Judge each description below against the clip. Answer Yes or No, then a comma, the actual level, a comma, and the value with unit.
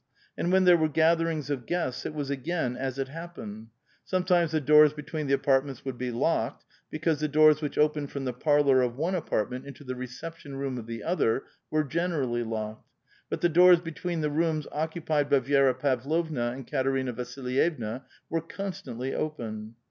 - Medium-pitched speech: Yes, medium, 145 Hz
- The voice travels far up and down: No, average, 4.0 semitones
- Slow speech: No, average, 180 wpm